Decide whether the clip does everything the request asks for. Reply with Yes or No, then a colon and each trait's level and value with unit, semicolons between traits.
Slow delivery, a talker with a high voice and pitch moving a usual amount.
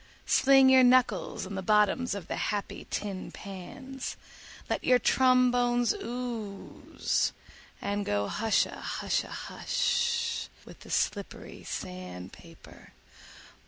Yes: slow, 105 wpm; high, 230 Hz; average, 4.4 semitones